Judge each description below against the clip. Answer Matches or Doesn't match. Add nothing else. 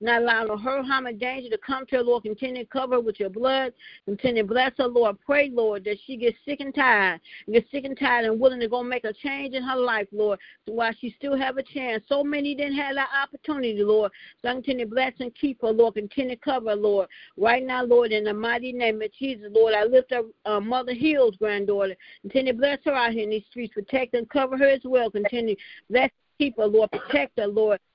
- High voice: Matches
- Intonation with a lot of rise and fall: Doesn't match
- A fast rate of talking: Matches